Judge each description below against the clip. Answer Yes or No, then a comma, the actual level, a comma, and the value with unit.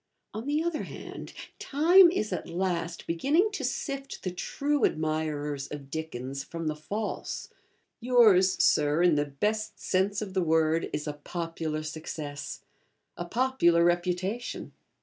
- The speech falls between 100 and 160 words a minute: Yes, average, 140 wpm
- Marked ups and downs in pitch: Yes, wide, 6.7 semitones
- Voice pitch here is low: No, medium, 175 Hz